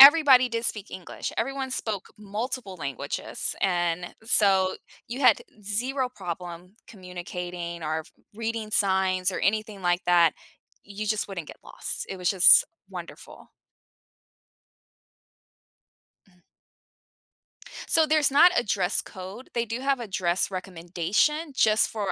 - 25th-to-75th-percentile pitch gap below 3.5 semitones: No, average, 4.7 semitones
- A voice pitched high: Yes, high, 200 Hz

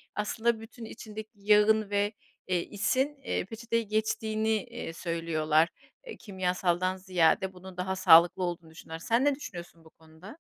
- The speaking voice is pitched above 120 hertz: Yes, high, 190 Hz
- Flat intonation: No, average, 4.1 semitones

